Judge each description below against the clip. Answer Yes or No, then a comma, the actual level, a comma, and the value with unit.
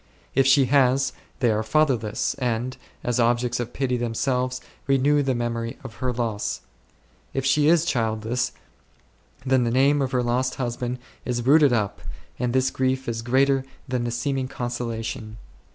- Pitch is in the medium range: No, low, 125 Hz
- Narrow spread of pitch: Yes, narrow, 2.0 semitones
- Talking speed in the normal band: Yes, average, 160 wpm